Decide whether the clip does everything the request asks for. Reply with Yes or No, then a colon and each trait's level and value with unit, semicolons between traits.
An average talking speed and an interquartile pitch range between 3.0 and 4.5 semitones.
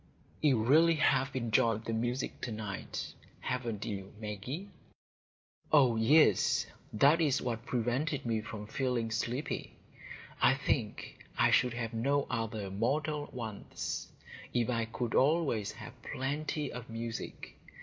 No: slow, 130 wpm; average, 3.7 semitones